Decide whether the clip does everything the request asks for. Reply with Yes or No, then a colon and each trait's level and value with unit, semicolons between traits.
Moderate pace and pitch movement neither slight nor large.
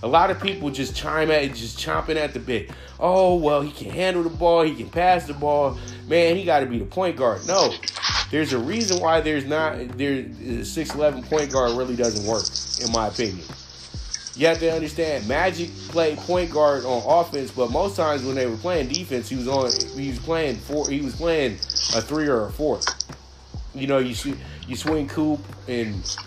No: fast, 210 wpm; average, 4.8 semitones